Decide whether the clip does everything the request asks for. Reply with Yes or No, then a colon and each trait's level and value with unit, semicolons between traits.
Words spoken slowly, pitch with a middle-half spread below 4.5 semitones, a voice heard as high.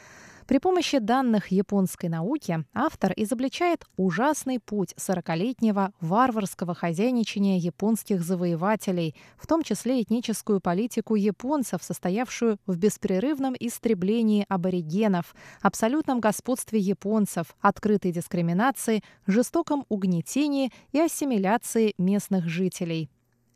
No: slow, 90 wpm; average, 4.8 semitones; high, 210 Hz